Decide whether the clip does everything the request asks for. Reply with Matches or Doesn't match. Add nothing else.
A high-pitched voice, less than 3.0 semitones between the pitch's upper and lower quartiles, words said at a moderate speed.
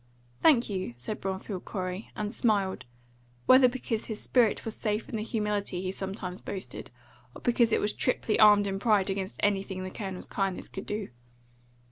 Matches